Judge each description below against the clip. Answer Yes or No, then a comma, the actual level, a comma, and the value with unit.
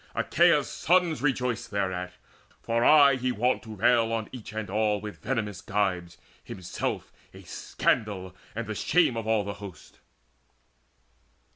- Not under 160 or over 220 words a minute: No, average, 140 wpm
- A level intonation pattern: No, average, 3.6 semitones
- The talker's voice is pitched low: Yes, low, 110 Hz